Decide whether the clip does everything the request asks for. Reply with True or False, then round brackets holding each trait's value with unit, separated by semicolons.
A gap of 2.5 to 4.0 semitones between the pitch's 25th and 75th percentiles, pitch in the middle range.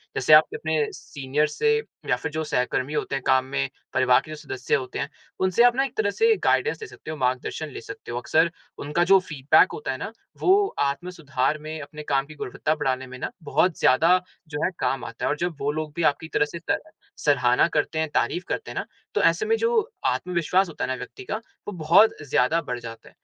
False (4.8 semitones; 155 Hz)